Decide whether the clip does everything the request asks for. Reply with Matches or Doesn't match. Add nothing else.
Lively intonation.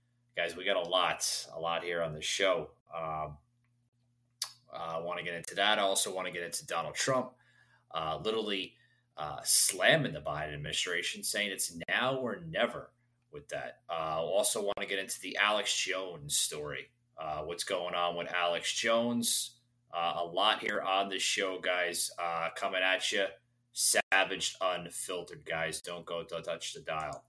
Matches